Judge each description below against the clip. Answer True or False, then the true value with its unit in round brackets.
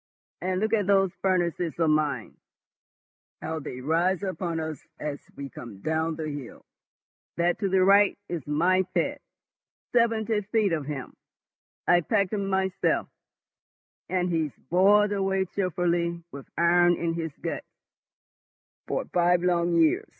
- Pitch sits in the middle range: True (175 Hz)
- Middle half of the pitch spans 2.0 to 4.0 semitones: True (3.1 semitones)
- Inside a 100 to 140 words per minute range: True (135 wpm)